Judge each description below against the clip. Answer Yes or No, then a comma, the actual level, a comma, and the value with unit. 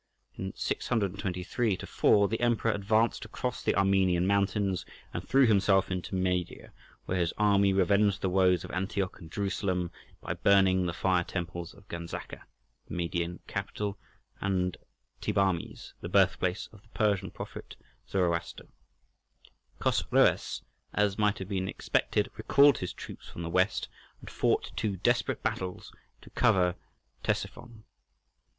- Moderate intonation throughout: No, narrow, 2.0 semitones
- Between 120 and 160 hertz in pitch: No, very low, 95 Hz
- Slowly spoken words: Yes, slow, 130 wpm